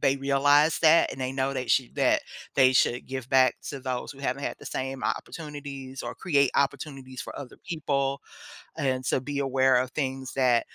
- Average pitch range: No, narrow, 1.4 semitones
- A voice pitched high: No, low, 135 Hz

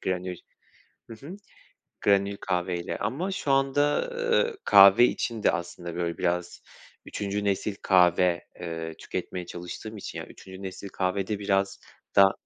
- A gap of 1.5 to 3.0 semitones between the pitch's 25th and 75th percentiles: No, average, 3.5 semitones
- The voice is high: No, very low, 95 Hz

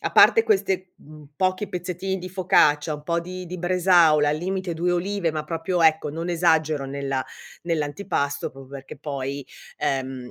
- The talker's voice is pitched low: No, medium, 165 Hz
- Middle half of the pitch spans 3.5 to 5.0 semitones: Yes, average, 3.8 semitones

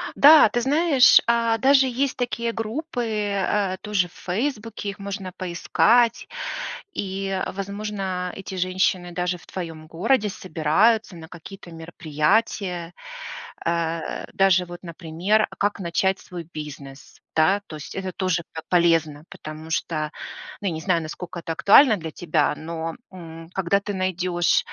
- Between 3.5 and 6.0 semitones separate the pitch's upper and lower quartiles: Yes, average, 3.9 semitones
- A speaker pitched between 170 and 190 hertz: Yes, medium, 185 Hz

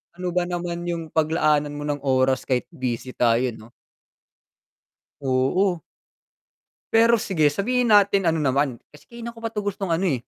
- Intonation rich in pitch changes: Yes, wide, 6.6 semitones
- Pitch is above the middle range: No, medium, 165 Hz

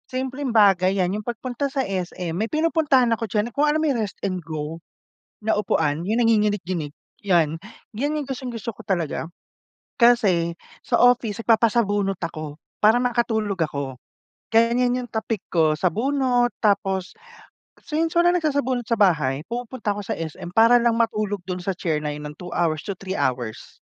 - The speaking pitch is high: Yes, high, 210 Hz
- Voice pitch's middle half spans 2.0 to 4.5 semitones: No, wide, 5.6 semitones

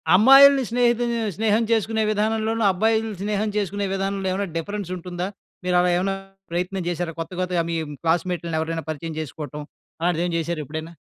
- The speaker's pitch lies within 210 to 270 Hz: No, medium, 185 Hz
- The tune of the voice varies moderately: Yes, average, 4.4 semitones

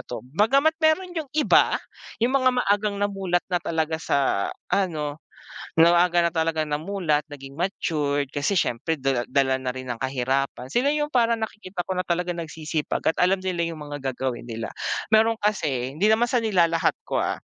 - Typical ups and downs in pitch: No, wide, 6.4 semitones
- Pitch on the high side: No, medium, 170 Hz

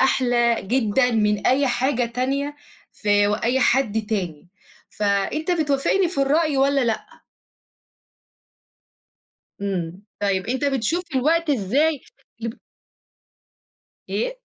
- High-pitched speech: Yes, very high, 250 Hz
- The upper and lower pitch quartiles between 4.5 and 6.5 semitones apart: Yes, average, 5.1 semitones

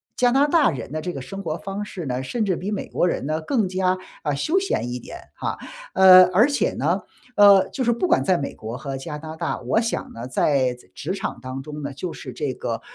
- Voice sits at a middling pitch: Yes, medium, 175 Hz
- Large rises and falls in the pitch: Yes, wide, 6.7 semitones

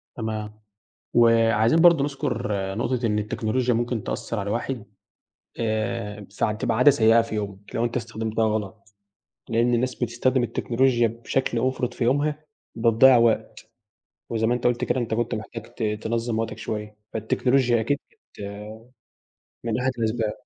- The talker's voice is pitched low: Yes, low, 115 Hz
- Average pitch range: No, narrow, 2.0 semitones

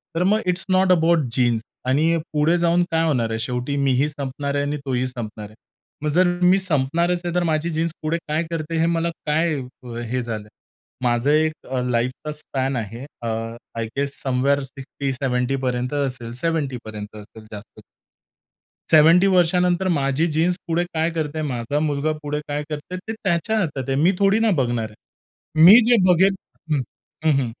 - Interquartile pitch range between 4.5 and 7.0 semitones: Yes, average, 4.8 semitones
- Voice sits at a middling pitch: Yes, medium, 145 Hz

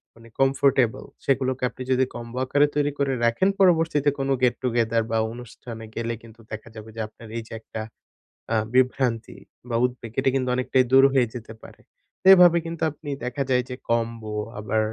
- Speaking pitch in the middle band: No, low, 125 Hz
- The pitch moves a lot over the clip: No, average, 2.9 semitones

